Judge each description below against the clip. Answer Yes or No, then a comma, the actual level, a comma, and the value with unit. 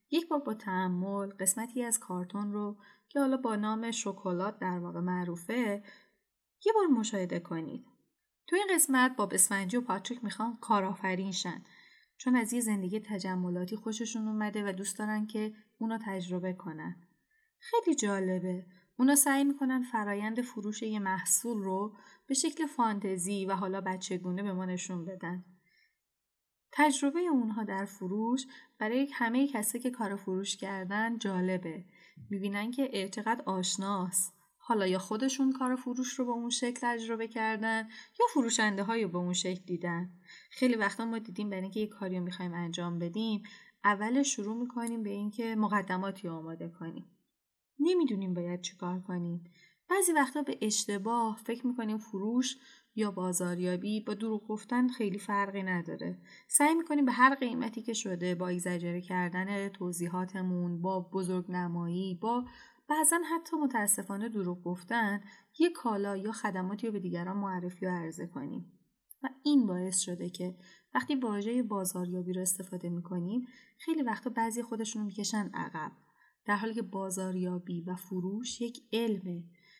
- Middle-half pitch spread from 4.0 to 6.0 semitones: Yes, average, 4.3 semitones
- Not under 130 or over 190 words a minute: Yes, average, 145 wpm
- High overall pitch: Yes, high, 205 Hz